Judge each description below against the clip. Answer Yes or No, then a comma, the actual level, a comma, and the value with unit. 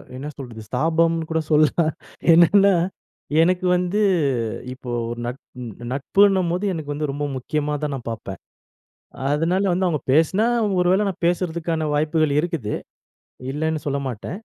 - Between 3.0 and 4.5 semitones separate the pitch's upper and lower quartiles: Yes, average, 3.6 semitones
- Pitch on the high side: No, medium, 160 Hz